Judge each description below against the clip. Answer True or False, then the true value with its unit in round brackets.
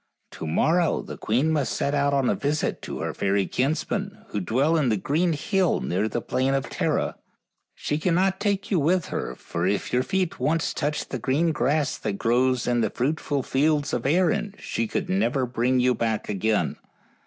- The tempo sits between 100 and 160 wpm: False (195 wpm)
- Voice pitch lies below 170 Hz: True (140 Hz)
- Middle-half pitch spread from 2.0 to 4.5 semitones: False (5.3 semitones)